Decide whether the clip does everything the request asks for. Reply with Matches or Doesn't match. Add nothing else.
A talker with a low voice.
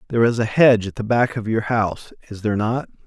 Matches